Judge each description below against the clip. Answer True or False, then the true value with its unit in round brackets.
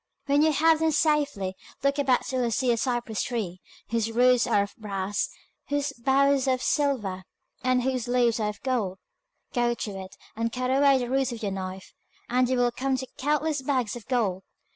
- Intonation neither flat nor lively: True (3.7 semitones)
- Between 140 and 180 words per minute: False (200 wpm)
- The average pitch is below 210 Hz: False (250 Hz)